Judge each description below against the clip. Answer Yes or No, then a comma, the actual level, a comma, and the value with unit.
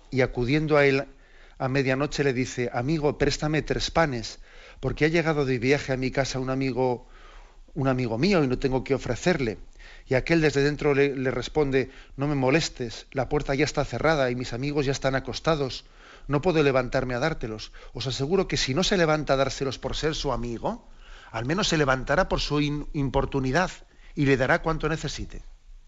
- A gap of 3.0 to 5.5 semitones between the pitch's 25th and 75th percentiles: No, narrow, 2.6 semitones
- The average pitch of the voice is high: No, medium, 140 Hz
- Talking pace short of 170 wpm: No, fast, 190 wpm